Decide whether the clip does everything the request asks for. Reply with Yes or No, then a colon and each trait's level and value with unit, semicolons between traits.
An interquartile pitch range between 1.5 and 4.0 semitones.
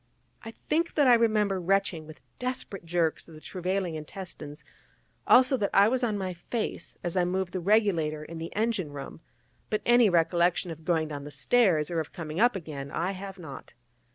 No: average, 4.6 semitones